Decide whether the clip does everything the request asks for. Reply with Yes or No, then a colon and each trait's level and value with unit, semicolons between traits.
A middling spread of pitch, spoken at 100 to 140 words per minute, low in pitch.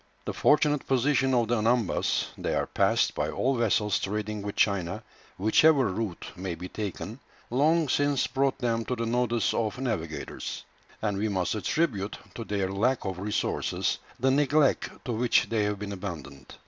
No: average, 4.6 semitones; average, 165 wpm; low, 110 Hz